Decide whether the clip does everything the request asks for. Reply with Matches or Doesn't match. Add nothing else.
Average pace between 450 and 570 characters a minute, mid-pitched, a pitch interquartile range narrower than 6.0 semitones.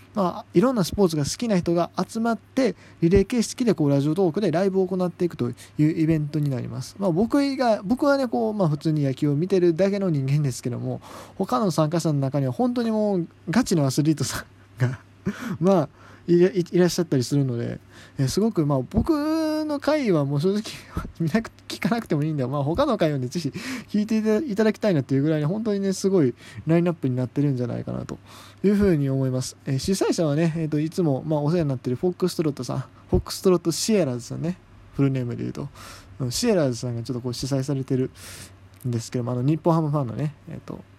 Doesn't match